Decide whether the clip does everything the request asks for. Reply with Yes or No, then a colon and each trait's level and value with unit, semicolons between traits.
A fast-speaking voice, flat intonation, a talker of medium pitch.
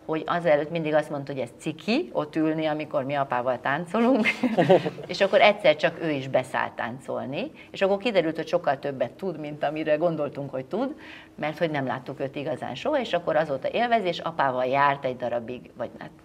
No: fast, 190 wpm; average, 5.0 semitones; medium, 155 Hz